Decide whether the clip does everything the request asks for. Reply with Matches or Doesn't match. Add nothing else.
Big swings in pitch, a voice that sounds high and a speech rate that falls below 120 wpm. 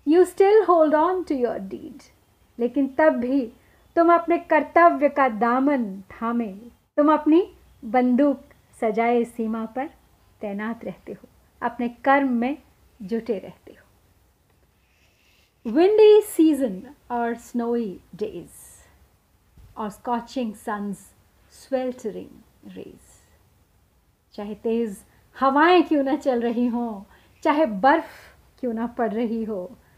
Matches